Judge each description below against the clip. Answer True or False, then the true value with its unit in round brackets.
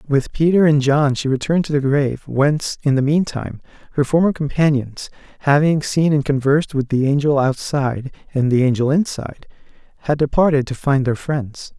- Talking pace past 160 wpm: True (180 wpm)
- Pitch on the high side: False (140 Hz)